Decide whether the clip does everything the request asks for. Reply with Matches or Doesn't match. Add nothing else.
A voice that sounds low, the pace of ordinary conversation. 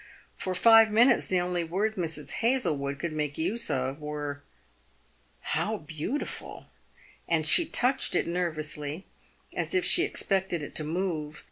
Doesn't match